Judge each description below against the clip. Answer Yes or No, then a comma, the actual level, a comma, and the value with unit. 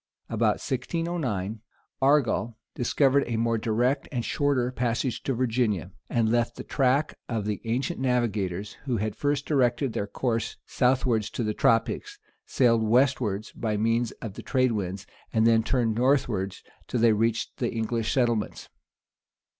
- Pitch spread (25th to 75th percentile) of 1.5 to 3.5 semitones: Yes, average, 2.7 semitones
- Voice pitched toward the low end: Yes, low, 120 Hz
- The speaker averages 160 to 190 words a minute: No, average, 145 wpm